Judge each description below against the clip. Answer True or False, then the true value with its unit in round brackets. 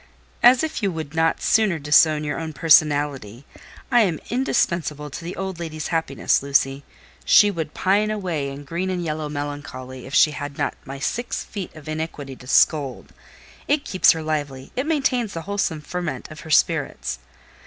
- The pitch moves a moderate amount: True (4.6 semitones)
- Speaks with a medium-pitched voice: True (155 Hz)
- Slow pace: False (170 wpm)